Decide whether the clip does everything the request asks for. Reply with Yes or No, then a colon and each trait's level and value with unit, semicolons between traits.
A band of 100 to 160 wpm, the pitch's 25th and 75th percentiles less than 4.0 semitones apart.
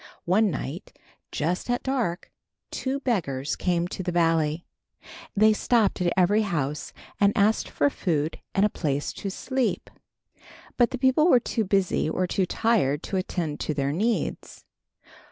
No: average, 155 wpm; wide, 5.5 semitones